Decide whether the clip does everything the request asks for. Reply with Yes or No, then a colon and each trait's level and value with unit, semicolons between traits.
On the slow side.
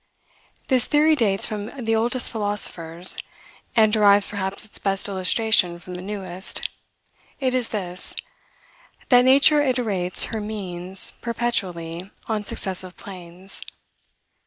Yes: slow, 115 wpm